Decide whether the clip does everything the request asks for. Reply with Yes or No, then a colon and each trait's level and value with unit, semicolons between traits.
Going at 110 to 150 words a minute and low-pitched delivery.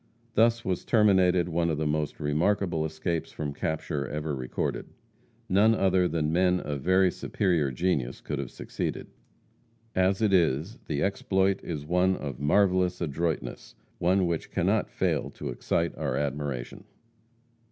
Yes: average, 140 wpm; very low, 85 Hz